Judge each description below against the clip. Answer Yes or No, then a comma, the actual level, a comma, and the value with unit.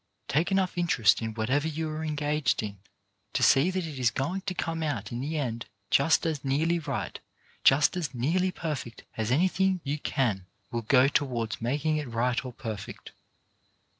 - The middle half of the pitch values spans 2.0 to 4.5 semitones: No, average, 5.1 semitones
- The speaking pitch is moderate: Yes, medium, 145 Hz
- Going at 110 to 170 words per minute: No, average, 180 wpm